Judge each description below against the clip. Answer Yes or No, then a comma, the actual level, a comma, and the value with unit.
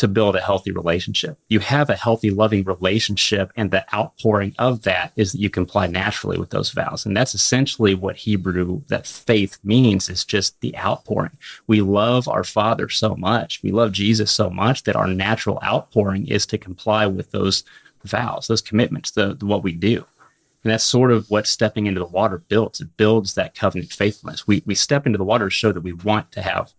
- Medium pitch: No, low, 105 Hz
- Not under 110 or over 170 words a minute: No, fast, 205 wpm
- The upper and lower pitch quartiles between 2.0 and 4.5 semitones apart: Yes, average, 2.7 semitones